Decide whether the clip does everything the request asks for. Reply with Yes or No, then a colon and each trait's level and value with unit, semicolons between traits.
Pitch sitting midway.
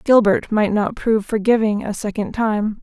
No: high, 215 Hz